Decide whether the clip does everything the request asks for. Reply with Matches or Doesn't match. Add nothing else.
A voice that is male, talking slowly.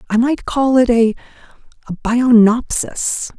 Doesn't match